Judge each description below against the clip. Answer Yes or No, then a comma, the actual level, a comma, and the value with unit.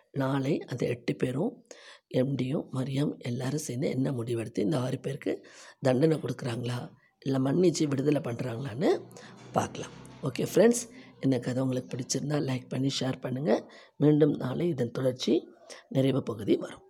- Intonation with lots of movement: No, narrow, 2.4 semitones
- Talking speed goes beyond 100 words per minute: Yes, fast, 130 wpm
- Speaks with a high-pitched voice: No, low, 135 Hz